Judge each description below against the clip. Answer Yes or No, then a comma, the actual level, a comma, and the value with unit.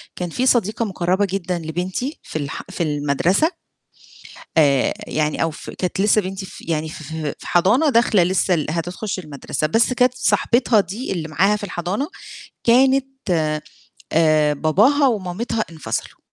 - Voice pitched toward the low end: No, medium, 185 Hz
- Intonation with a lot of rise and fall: Yes, wide, 5.7 semitones